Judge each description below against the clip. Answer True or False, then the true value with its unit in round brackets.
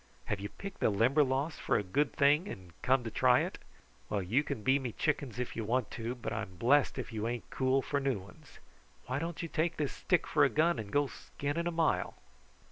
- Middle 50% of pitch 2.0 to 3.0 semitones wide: False (4.6 semitones)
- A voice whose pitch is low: True (130 Hz)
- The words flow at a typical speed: False (225 wpm)